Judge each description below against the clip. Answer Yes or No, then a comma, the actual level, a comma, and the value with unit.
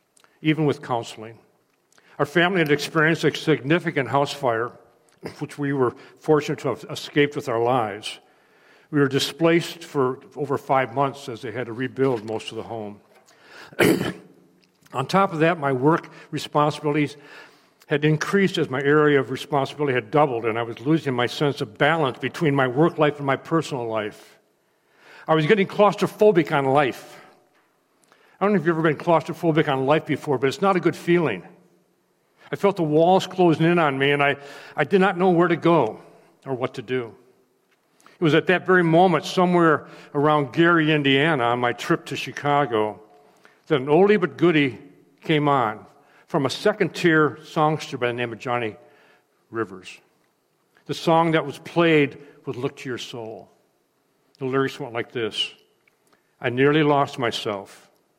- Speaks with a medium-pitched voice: Yes, medium, 145 Hz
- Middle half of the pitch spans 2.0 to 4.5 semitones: Yes, average, 3.6 semitones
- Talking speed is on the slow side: No, average, 170 wpm